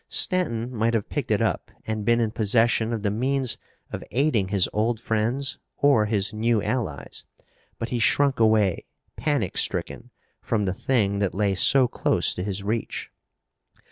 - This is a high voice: No, low, 110 Hz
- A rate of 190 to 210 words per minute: No, average, 165 wpm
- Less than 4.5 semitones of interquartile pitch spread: Yes, average, 2.9 semitones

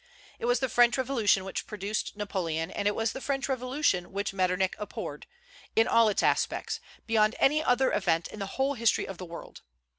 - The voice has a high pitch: Yes, high, 215 Hz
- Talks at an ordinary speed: Yes, average, 190 wpm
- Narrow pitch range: No, average, 4.5 semitones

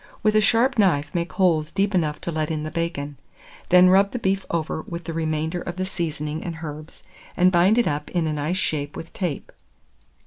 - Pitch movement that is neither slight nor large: Yes, average, 3.4 semitones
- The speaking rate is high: Yes, fast, 210 wpm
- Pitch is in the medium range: Yes, medium, 170 Hz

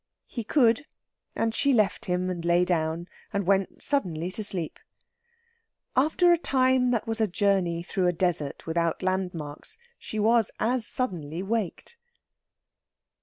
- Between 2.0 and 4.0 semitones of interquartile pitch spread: No, average, 5.1 semitones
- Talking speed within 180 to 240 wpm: No, average, 140 wpm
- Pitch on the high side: Yes, high, 195 Hz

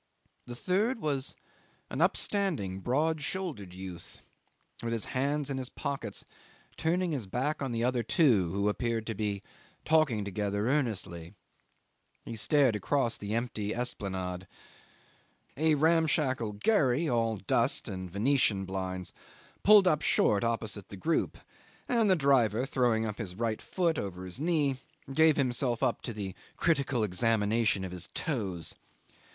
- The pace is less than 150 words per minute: Yes, average, 140 wpm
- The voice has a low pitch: Yes, low, 120 Hz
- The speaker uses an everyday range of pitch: No, wide, 6.4 semitones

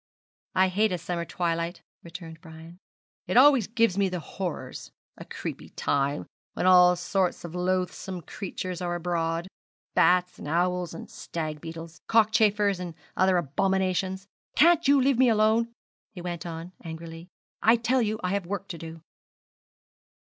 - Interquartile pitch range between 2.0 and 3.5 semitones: Yes, average, 3.1 semitones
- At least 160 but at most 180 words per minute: No, average, 150 wpm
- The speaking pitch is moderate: Yes, medium, 180 Hz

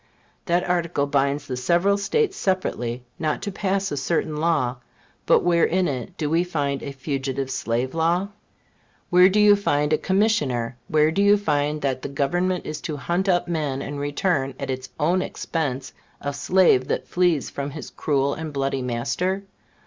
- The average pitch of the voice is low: No, medium, 150 Hz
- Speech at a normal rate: Yes, average, 170 wpm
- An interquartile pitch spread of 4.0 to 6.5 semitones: Yes, average, 4.7 semitones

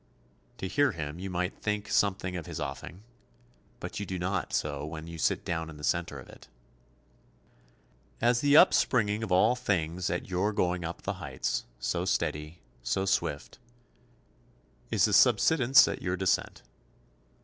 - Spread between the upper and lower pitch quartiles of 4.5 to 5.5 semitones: No, average, 4.0 semitones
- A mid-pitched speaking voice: No, very low, 90 Hz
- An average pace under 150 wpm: No, average, 160 wpm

